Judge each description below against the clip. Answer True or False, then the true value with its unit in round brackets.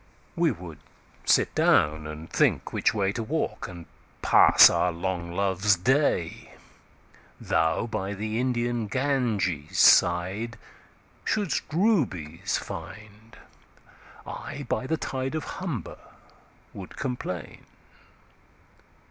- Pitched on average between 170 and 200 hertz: False (105 Hz)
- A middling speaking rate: False (90 wpm)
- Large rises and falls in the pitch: True (6.8 semitones)